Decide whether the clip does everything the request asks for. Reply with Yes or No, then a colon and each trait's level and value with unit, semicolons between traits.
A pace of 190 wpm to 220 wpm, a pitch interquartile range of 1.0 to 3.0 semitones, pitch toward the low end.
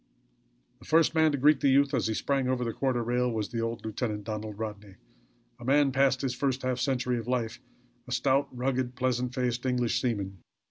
Yes: average, 200 wpm; narrow, 2.6 semitones; low, 125 Hz